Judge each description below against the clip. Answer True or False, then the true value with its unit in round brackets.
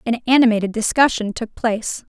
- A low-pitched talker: False (230 Hz)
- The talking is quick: False (140 wpm)